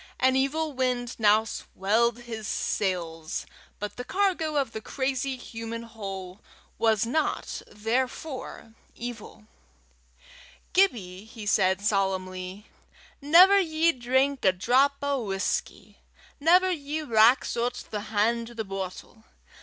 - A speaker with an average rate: No, slow, 120 wpm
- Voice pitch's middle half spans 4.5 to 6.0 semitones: Yes, average, 4.8 semitones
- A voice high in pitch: Yes, high, 235 Hz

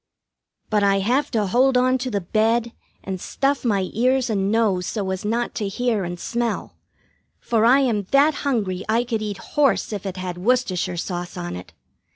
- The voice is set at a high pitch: Yes, high, 215 Hz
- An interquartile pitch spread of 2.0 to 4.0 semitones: No, average, 4.6 semitones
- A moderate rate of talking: Yes, average, 190 wpm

